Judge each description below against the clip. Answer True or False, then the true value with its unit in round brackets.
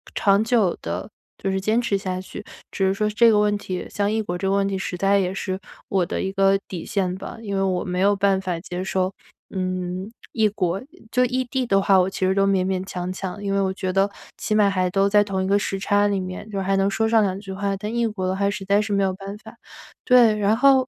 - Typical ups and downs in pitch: False (1.7 semitones)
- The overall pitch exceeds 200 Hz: False (195 Hz)